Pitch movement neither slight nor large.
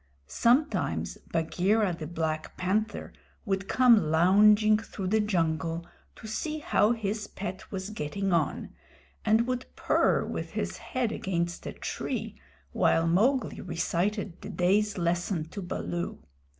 Yes: average, 4.0 semitones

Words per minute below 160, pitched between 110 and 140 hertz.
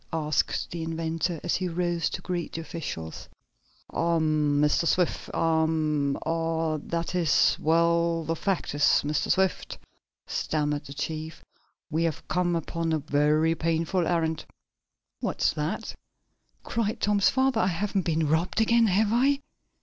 No: average, 140 wpm; medium, 165 Hz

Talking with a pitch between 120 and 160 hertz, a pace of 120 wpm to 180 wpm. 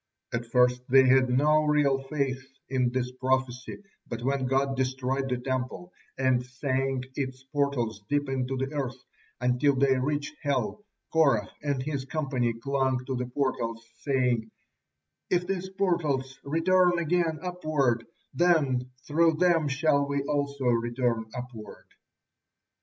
Yes: low, 135 Hz; slow, 135 wpm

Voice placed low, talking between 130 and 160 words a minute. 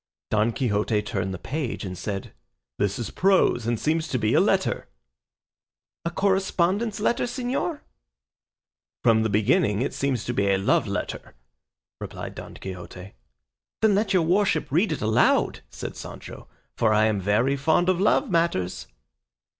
Yes: low, 125 Hz; average, 155 wpm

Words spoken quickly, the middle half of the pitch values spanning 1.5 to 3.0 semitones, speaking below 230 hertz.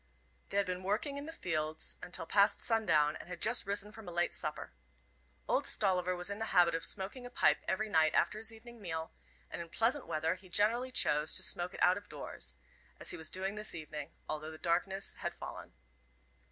No: fast, 210 wpm; average, 4.4 semitones; medium, 185 Hz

